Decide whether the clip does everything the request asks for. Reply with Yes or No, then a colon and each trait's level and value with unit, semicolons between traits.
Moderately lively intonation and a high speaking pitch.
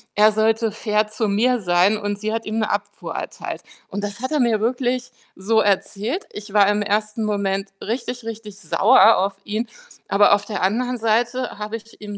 No: narrow, 1.9 semitones; high, 215 Hz